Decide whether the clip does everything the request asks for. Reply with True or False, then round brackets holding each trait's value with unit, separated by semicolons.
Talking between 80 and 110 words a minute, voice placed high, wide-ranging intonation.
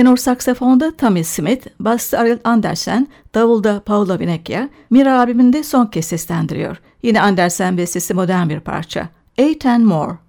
False (140 wpm; 225 Hz; 5.9 semitones)